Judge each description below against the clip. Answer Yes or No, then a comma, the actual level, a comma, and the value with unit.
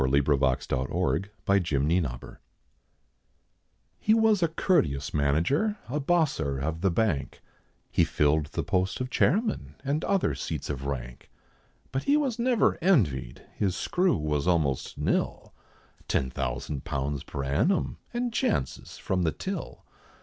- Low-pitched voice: Yes, very low, 80 Hz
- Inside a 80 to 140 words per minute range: Yes, slow, 135 wpm